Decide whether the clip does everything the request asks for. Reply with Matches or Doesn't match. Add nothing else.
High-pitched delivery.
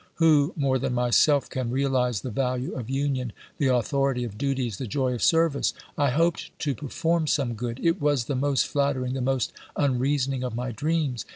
Doesn't match